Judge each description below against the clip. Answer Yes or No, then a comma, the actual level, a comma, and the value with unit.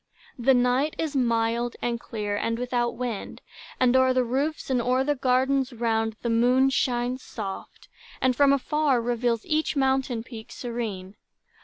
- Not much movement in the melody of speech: Yes, narrow, 2.3 semitones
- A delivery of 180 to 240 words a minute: No, average, 155 wpm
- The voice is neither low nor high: No, high, 245 Hz